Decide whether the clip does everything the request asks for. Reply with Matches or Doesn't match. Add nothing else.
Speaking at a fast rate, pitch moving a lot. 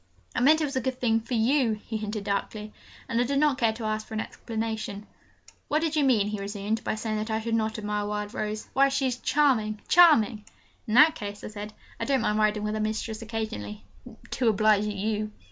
Doesn't match